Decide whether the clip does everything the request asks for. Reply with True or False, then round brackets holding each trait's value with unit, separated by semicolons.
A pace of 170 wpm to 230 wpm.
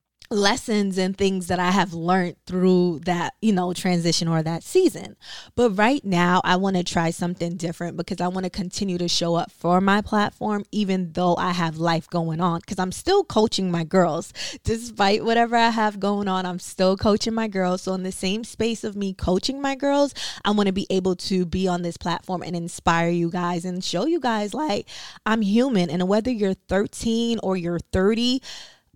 True (200 wpm)